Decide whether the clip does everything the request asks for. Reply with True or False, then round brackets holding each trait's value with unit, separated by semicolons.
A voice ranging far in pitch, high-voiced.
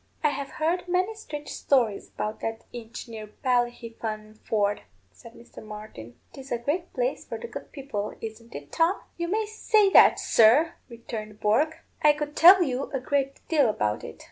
True (6.6 semitones; 255 Hz)